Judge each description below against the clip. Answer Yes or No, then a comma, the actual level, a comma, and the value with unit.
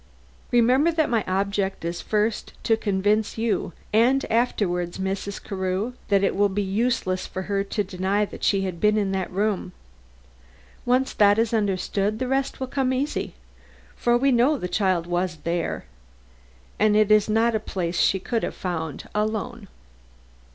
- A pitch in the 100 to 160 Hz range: No, high, 205 Hz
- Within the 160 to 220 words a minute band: Yes, average, 165 wpm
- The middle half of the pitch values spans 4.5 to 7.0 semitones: No, average, 3.3 semitones